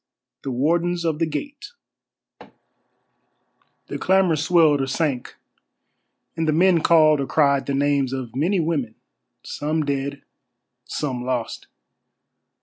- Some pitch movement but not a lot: Yes, average, 3.4 semitones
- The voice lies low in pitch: No, medium, 150 Hz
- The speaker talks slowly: Yes, slow, 120 wpm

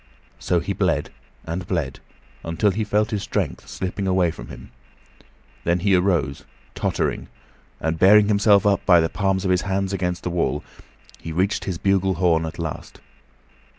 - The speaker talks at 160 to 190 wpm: Yes, average, 165 wpm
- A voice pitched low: Yes, very low, 95 Hz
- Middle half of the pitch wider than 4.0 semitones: No, average, 2.9 semitones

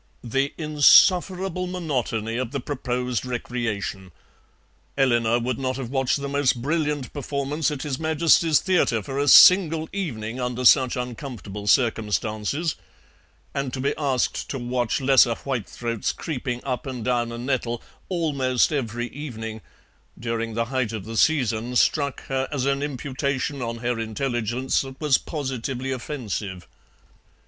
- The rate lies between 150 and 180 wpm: No, average, 140 wpm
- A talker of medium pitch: No, low, 130 Hz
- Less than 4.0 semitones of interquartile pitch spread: Yes, average, 3.3 semitones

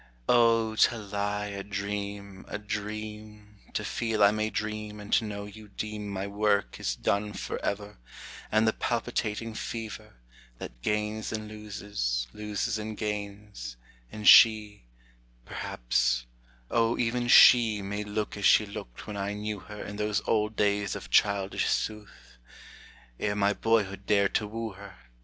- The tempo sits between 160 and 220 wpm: No, average, 145 wpm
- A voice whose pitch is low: Yes, low, 105 Hz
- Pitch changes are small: Yes, narrow, 1.1 semitones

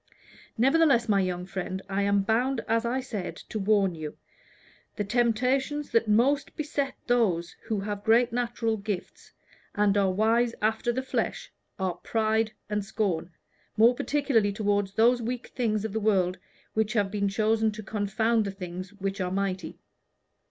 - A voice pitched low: No, high, 215 Hz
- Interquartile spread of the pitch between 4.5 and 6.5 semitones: No, average, 3.1 semitones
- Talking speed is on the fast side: No, average, 160 wpm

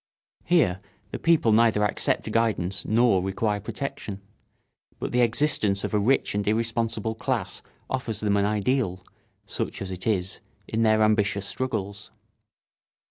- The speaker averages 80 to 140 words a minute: Yes, slow, 135 wpm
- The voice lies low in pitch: Yes, low, 110 Hz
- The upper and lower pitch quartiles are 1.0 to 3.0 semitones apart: Yes, narrow, 2.5 semitones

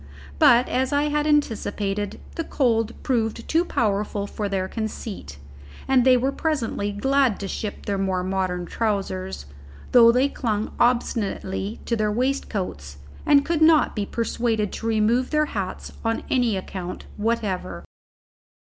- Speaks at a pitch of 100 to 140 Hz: No, high, 225 Hz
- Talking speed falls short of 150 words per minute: Yes, average, 140 wpm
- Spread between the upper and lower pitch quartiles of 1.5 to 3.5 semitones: No, average, 4.4 semitones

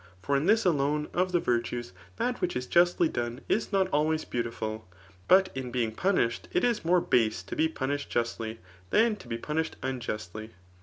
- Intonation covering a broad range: Yes, wide, 7.0 semitones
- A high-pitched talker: No, medium, 140 Hz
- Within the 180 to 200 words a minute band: Yes, average, 190 wpm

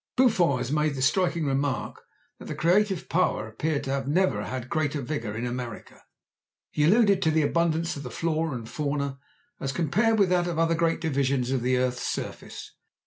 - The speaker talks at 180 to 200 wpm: Yes, average, 190 wpm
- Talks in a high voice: No, medium, 150 Hz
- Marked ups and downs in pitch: No, average, 4.2 semitones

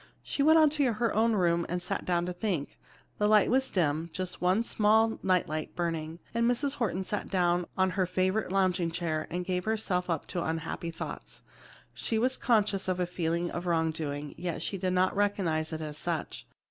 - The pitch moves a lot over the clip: No, average, 3.8 semitones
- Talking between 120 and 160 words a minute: No, average, 200 wpm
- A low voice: No, medium, 180 Hz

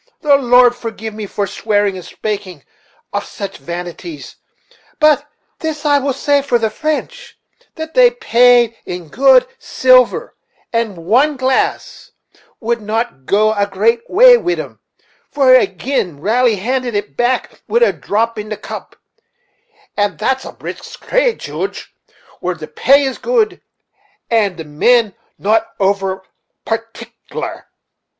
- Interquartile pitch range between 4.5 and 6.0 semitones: Yes, average, 5.2 semitones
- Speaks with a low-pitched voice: No, high, 235 Hz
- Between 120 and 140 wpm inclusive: Yes, slow, 135 wpm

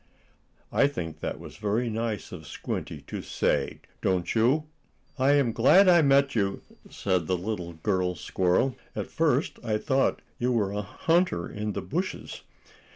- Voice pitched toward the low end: Yes, low, 110 Hz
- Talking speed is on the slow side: No, average, 160 wpm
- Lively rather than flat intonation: Yes, wide, 6.5 semitones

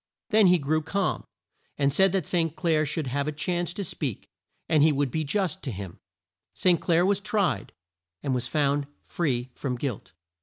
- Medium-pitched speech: Yes, medium, 155 Hz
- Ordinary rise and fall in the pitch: Yes, average, 4.3 semitones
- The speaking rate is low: No, average, 185 wpm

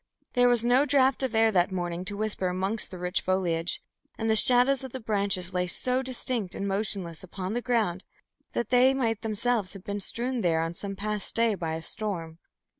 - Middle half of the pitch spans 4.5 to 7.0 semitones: Yes, average, 4.8 semitones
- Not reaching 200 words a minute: No, fast, 205 wpm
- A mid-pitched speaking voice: No, high, 205 Hz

